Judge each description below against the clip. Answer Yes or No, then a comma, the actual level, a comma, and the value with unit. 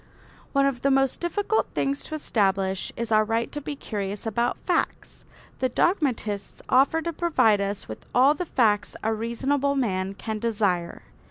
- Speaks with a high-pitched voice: Yes, high, 235 Hz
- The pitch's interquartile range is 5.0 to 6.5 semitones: Yes, average, 5.3 semitones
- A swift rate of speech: No, average, 165 wpm